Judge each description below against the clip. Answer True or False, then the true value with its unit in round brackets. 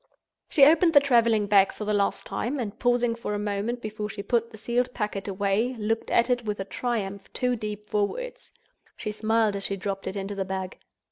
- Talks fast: True (215 wpm)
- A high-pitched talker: True (215 Hz)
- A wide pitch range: False (3.1 semitones)